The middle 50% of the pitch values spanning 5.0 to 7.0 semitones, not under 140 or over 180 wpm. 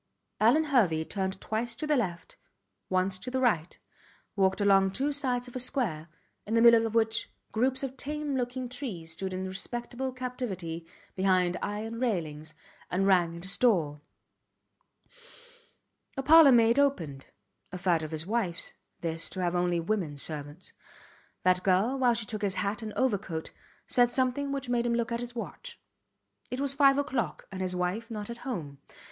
Yes: wide, 5.6 semitones; average, 170 wpm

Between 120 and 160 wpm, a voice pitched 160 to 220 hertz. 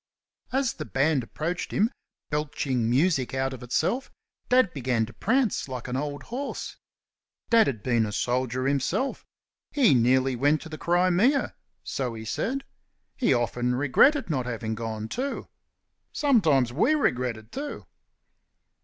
No: average, 140 wpm; low, 135 Hz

